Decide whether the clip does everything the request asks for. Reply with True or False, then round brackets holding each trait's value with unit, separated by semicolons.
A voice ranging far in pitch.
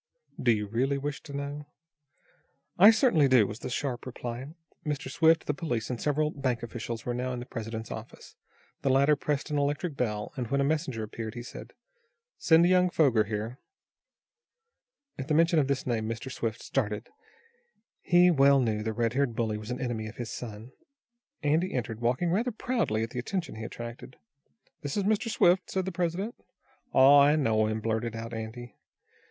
False (4.8 semitones)